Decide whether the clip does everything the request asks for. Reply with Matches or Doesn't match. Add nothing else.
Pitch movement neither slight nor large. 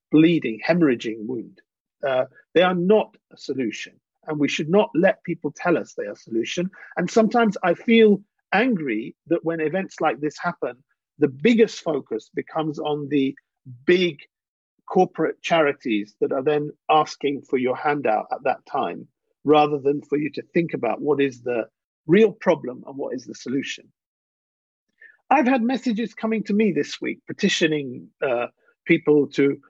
Doesn't match